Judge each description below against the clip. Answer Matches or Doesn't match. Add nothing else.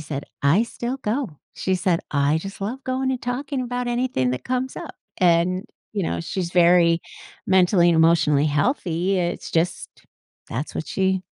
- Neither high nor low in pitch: Matches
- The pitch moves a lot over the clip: Matches